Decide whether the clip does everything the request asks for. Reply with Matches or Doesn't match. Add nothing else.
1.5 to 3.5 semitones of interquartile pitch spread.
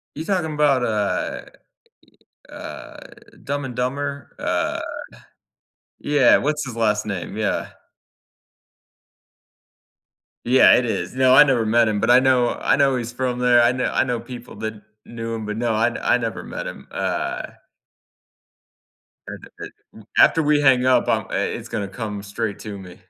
Matches